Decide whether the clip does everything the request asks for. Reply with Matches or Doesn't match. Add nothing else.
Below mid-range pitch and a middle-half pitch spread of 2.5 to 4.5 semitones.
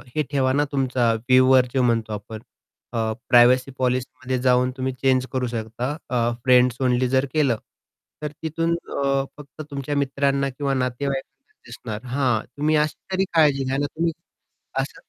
Doesn't match